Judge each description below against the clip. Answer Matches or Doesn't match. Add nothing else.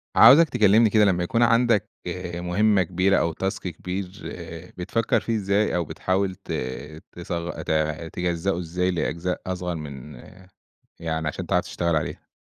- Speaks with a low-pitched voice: Matches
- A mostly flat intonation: Doesn't match